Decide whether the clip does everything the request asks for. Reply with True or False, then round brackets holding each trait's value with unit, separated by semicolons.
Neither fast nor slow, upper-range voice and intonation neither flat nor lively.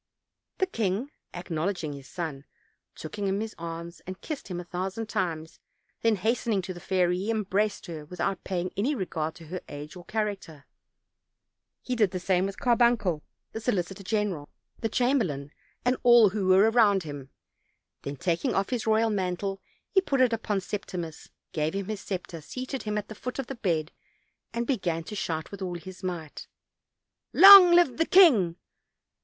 True (175 wpm; 195 Hz; 4.6 semitones)